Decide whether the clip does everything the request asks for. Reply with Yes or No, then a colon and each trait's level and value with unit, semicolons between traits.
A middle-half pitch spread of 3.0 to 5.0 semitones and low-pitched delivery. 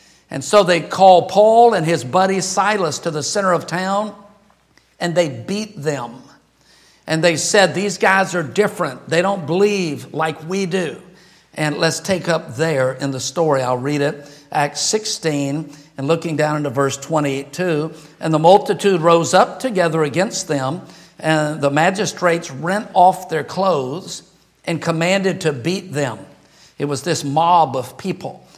No: average, 4.1 semitones; medium, 170 Hz